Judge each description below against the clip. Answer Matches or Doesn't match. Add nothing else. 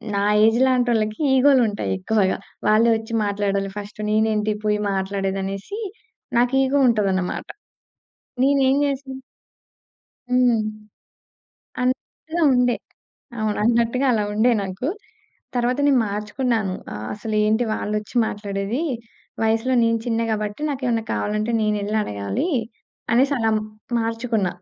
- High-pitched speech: Matches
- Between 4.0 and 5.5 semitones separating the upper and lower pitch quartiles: Doesn't match